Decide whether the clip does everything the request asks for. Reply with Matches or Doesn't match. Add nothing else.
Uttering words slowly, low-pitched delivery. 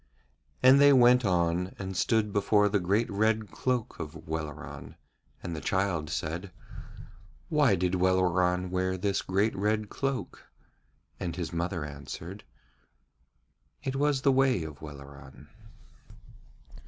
Matches